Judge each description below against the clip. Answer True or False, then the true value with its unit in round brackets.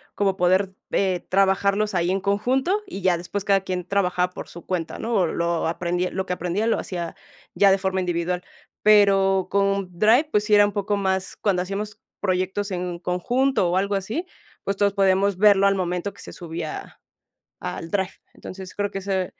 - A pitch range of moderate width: False (2.0 semitones)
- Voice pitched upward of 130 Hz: True (190 Hz)